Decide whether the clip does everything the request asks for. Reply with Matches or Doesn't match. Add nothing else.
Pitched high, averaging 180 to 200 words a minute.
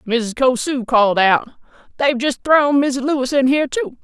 Matches